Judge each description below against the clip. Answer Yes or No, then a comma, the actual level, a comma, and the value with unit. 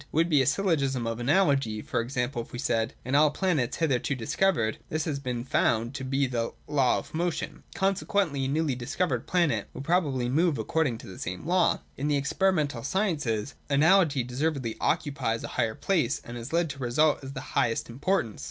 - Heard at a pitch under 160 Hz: Yes, medium, 140 Hz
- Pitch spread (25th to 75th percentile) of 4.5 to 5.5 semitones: Yes, average, 4.9 semitones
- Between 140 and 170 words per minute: No, average, 190 wpm